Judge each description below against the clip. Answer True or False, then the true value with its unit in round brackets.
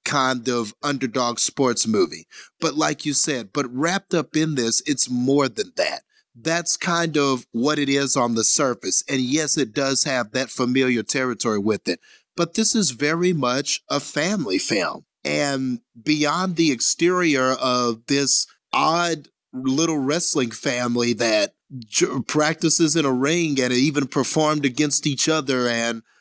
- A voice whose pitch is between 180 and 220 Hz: False (140 Hz)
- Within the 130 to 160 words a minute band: True (155 wpm)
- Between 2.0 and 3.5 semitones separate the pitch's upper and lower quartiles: False (4.1 semitones)